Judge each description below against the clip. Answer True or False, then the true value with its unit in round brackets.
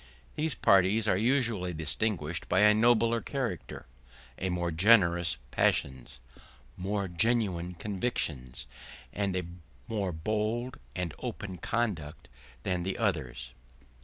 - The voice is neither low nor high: False (95 Hz)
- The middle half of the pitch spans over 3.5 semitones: True (4.6 semitones)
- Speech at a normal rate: False (110 wpm)